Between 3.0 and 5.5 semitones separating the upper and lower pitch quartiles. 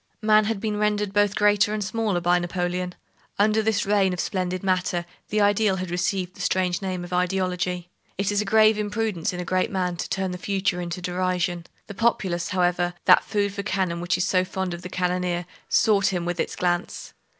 No: narrow, 2.4 semitones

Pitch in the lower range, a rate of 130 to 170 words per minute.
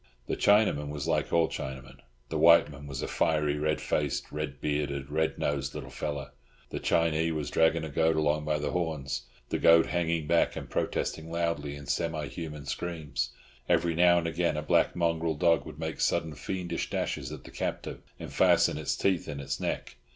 No: very low, 75 Hz; average, 190 wpm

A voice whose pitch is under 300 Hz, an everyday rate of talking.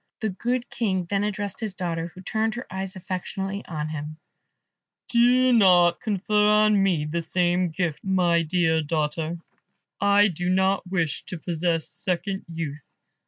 Yes: medium, 185 Hz; average, 150 wpm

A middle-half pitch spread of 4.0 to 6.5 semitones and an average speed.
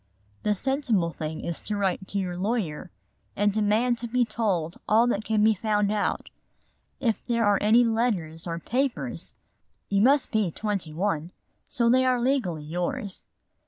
Yes: average, 4.7 semitones; average, 160 wpm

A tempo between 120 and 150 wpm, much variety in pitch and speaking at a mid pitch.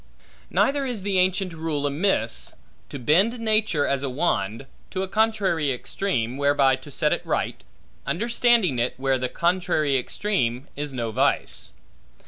Yes: average, 145 wpm; wide, 6.8 semitones; medium, 150 Hz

